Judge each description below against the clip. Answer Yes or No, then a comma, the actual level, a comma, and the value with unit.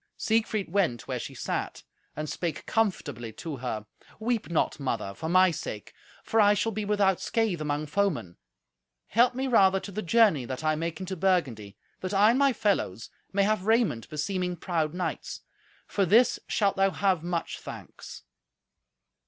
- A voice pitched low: No, medium, 185 Hz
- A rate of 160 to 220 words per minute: Yes, average, 165 wpm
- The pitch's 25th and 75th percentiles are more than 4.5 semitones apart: Yes, average, 5.3 semitones